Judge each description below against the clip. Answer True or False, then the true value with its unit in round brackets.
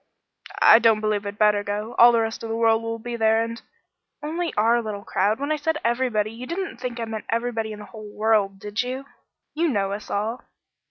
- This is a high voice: True (225 Hz)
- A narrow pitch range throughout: True (2.2 semitones)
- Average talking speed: False (225 wpm)